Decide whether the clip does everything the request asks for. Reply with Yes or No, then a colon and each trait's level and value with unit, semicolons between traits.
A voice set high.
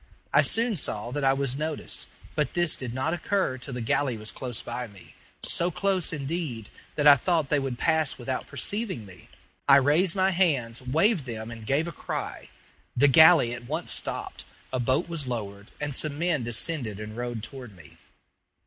No: low, 135 Hz